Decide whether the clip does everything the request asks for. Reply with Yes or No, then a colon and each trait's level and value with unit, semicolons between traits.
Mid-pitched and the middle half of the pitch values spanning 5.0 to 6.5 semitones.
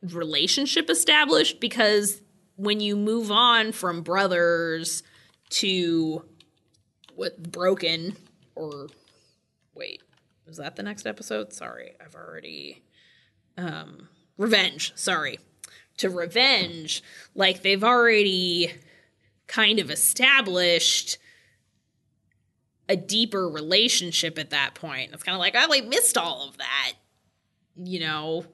No: medium, 180 Hz; average, 4.2 semitones